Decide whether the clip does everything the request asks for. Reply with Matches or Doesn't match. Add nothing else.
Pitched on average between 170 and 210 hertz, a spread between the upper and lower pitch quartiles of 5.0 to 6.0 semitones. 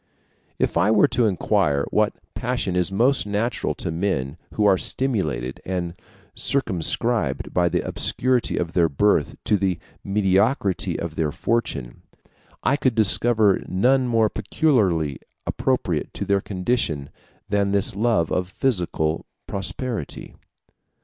Doesn't match